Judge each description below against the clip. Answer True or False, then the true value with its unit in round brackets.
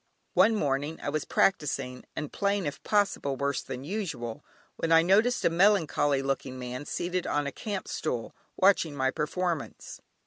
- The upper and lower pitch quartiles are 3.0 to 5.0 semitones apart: False (5.6 semitones)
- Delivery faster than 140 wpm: True (160 wpm)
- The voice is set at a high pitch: False (155 Hz)